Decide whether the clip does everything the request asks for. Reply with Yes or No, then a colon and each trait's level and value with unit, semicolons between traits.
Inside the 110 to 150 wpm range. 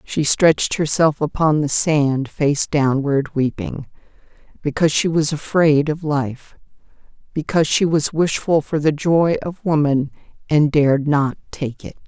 Yes: average, 140 wpm